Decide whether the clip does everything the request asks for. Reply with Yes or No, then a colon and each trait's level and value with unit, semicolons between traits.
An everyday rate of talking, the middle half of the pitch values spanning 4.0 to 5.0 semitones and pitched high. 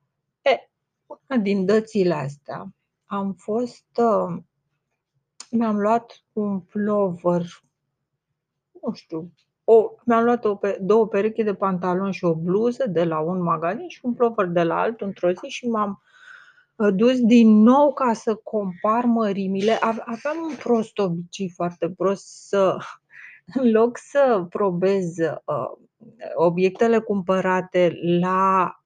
Yes: average, 125 wpm; average, 4.6 semitones; high, 200 Hz